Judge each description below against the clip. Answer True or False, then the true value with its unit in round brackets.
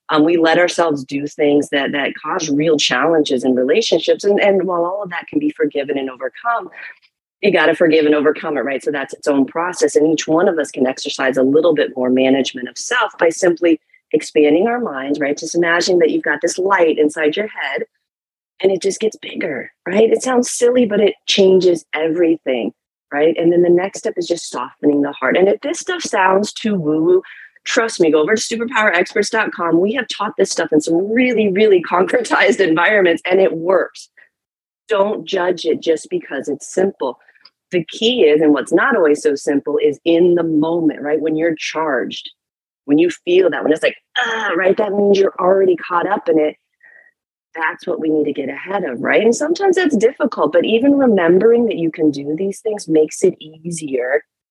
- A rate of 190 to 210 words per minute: True (200 wpm)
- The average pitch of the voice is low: False (175 Hz)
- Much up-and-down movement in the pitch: True (5.8 semitones)